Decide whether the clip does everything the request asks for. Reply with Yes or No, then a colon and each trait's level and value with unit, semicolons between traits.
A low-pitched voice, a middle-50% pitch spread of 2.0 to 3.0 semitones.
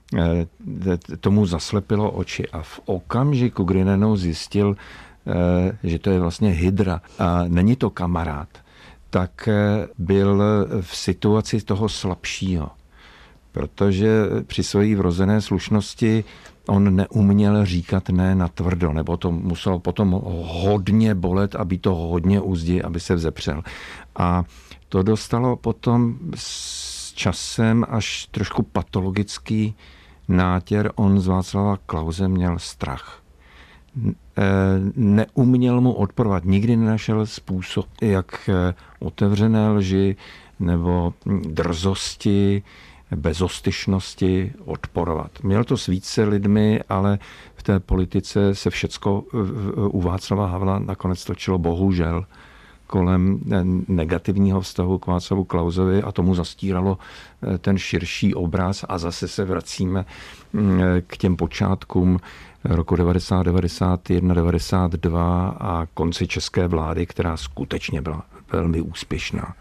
Yes: very low, 95 Hz; narrow, 2.6 semitones